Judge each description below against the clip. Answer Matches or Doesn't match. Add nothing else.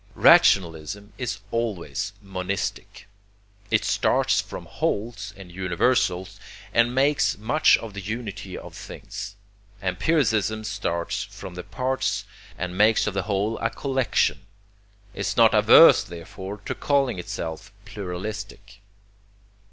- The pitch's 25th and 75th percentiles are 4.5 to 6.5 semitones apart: Doesn't match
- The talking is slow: Matches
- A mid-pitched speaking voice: Doesn't match